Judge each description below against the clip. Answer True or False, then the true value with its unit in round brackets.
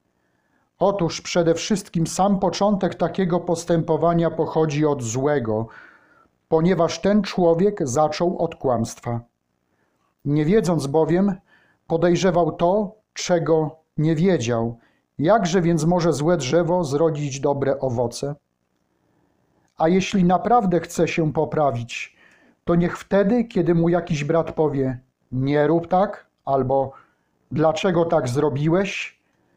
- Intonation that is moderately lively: True (3.6 semitones)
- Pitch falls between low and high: True (165 Hz)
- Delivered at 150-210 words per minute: False (110 wpm)